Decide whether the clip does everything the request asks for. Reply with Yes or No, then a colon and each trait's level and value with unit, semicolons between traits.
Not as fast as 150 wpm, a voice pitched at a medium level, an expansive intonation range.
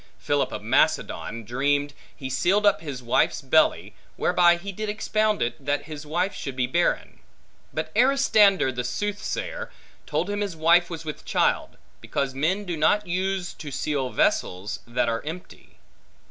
No: average, 160 wpm; medium, 165 Hz; wide, 6.7 semitones